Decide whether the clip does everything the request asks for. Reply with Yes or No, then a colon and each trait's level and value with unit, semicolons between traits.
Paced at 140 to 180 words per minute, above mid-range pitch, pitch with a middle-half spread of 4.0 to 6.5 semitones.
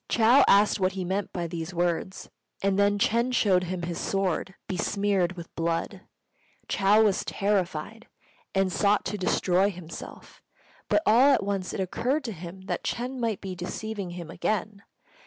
No: average, 160 wpm; high, 195 Hz; average, 2.8 semitones